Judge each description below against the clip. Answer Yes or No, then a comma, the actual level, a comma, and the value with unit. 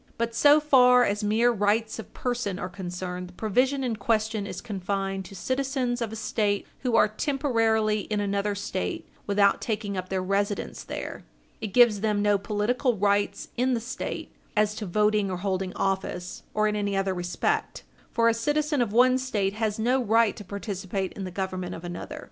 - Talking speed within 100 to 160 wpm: No, average, 185 wpm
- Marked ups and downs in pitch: No, average, 3.1 semitones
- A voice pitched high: Yes, high, 210 Hz